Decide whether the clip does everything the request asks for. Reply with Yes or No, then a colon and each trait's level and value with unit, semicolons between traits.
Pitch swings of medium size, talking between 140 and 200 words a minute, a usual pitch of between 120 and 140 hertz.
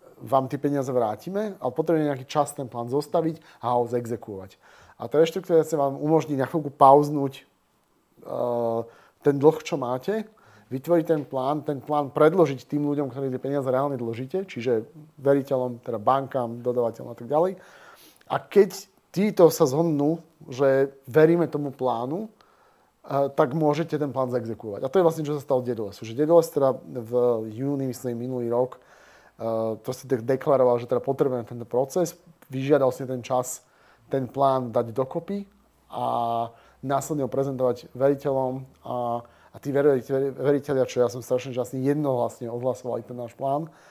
Yes: average, 3.5 semitones; fast, 165 wpm; low, 135 Hz